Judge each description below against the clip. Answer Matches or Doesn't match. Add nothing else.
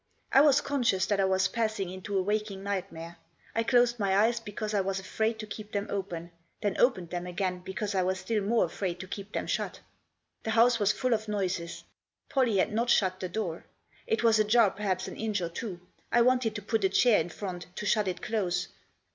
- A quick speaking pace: Matches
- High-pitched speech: Matches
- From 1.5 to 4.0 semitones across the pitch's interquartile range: Matches